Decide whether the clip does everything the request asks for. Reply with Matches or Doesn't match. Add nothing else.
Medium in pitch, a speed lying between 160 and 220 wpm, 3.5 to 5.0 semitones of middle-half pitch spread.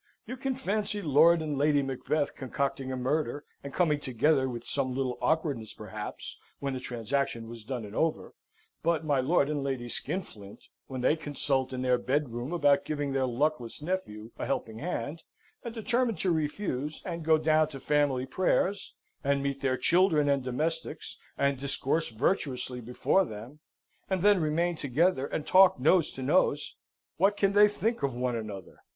Matches